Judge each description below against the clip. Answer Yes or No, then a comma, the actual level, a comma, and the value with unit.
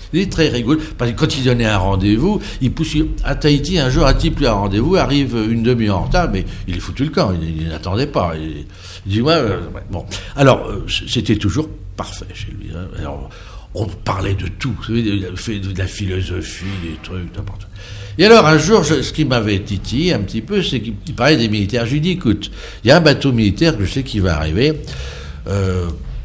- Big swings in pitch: Yes, wide, 6.9 semitones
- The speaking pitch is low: Yes, low, 105 Hz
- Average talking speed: No, fast, 225 wpm